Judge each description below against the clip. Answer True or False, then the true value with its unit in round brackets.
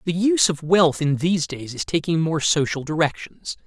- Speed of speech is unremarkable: True (195 wpm)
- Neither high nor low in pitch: True (160 Hz)